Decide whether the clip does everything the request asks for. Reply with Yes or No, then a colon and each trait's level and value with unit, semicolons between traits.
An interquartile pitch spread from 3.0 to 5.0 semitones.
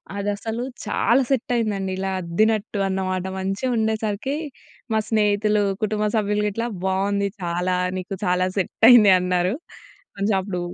No: narrow, 2.5 semitones